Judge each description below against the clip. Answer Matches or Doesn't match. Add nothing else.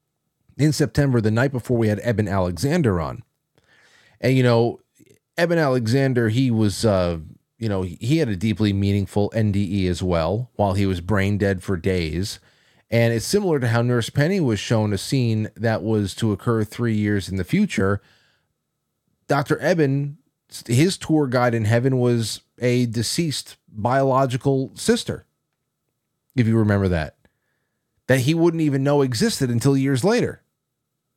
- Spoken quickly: Doesn't match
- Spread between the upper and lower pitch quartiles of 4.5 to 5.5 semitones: Matches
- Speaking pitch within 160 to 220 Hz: Doesn't match